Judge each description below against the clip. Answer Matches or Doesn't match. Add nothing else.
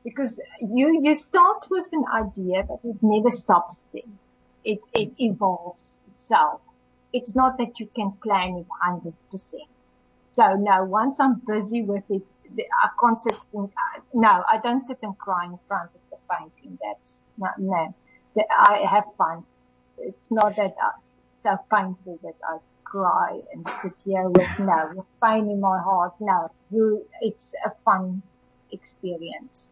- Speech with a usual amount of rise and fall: Matches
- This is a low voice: Doesn't match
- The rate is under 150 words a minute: Doesn't match